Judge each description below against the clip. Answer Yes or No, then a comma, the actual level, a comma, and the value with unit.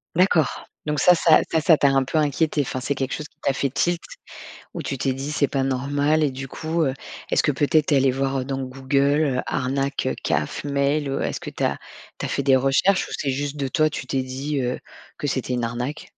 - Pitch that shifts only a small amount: Yes, narrow, 2.1 semitones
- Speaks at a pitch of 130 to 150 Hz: Yes, medium, 140 Hz